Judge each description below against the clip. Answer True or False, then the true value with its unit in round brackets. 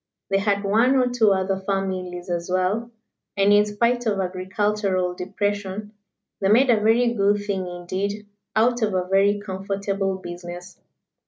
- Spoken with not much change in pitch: True (2.0 semitones)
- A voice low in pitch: False (200 Hz)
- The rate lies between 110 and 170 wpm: True (150 wpm)